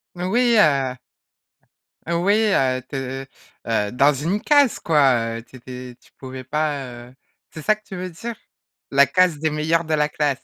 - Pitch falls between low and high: Yes, medium, 150 Hz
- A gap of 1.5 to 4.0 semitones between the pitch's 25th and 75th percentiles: No, average, 5.1 semitones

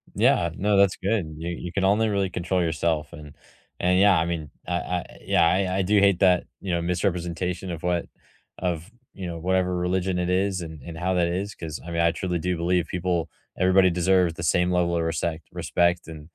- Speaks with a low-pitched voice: Yes, very low, 90 Hz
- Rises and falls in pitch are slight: Yes, narrow, 1.8 semitones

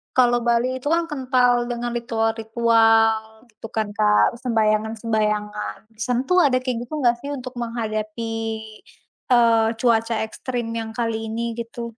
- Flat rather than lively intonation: Yes, narrow, 1.7 semitones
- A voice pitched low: No, high, 230 Hz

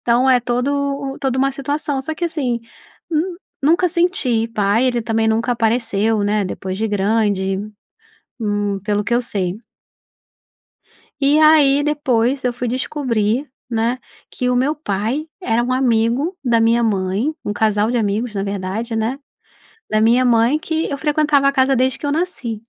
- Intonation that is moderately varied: Yes, average, 4.2 semitones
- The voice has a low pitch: No, high, 240 Hz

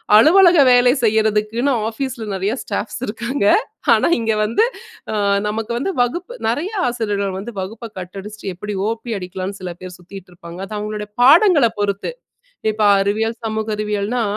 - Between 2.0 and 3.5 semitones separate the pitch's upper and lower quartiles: Yes, average, 3.2 semitones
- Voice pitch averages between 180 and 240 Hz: Yes, high, 220 Hz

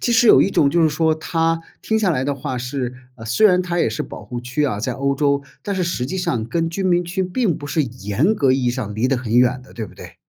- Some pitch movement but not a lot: No, wide, 5.8 semitones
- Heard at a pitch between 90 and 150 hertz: Yes, medium, 140 Hz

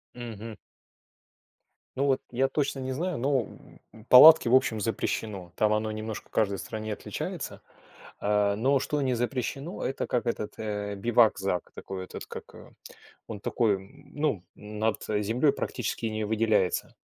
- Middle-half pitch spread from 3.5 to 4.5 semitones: Yes, average, 3.9 semitones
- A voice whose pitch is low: Yes, low, 110 Hz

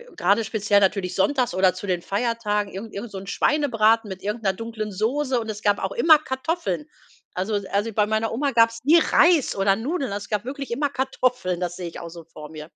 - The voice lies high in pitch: Yes, high, 215 Hz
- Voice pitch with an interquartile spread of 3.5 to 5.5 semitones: Yes, average, 4.4 semitones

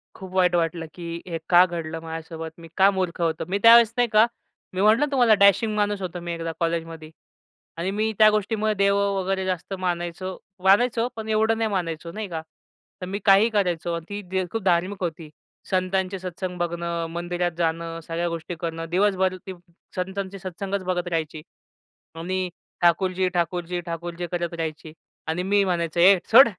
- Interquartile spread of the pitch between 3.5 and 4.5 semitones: No, average, 2.8 semitones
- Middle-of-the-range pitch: Yes, medium, 180 Hz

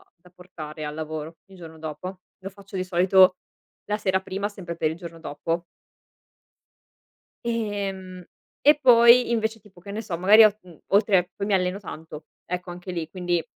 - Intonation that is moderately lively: Yes, average, 3.1 semitones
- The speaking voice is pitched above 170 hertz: Yes, medium, 185 Hz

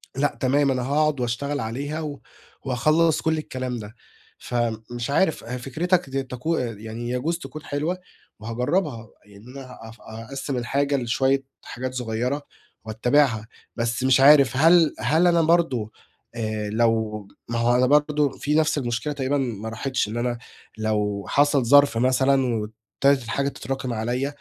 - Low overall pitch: Yes, low, 130 Hz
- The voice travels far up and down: No, average, 3.7 semitones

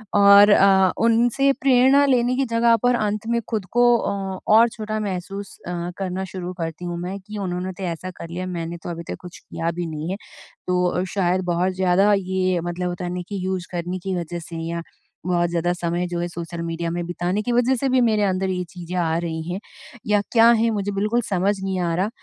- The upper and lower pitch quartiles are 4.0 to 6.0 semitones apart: No, average, 3.1 semitones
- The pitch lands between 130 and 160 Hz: No, medium, 185 Hz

